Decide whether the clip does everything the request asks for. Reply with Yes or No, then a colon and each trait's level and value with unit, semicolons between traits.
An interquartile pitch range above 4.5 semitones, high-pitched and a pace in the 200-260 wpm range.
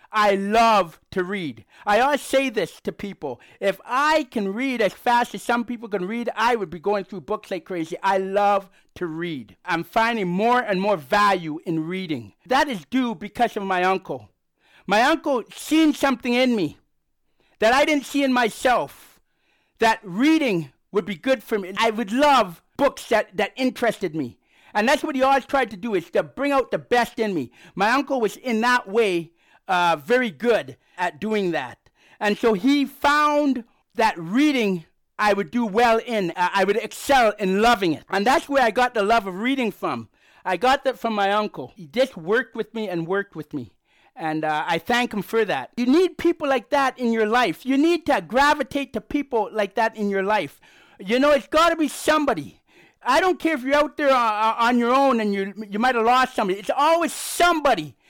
Yes: average, 5.2 semitones; high, 225 Hz; fast, 205 wpm